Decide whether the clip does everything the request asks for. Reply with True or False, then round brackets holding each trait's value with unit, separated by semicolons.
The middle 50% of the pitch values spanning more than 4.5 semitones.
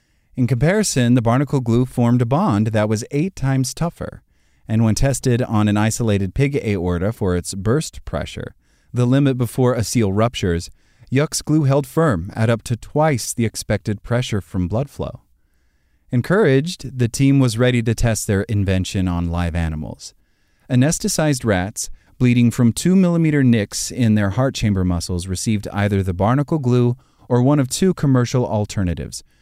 True (5.2 semitones)